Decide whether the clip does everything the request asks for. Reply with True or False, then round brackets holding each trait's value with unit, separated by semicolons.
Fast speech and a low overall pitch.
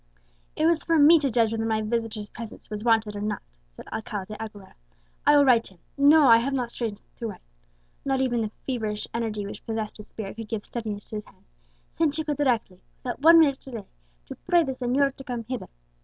False (220 wpm; 230 Hz)